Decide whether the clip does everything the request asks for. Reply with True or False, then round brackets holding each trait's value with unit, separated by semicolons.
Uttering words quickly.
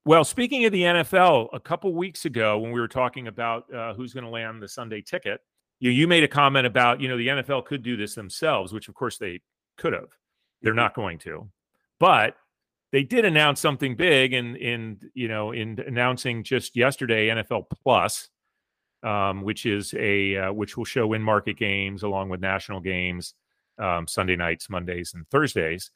False (190 wpm)